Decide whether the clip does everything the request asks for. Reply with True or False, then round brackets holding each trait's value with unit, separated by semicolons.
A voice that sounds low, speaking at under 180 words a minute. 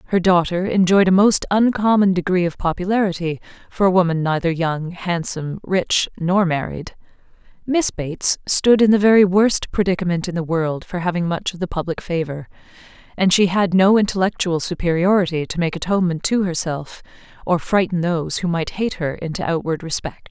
False (180 Hz; 170 wpm)